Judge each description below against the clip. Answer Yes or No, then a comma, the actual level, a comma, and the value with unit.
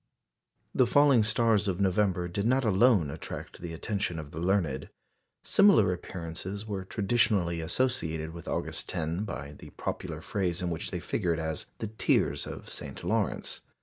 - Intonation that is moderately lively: Yes, average, 4.6 semitones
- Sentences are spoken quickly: No, average, 155 wpm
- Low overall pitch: Yes, very low, 95 Hz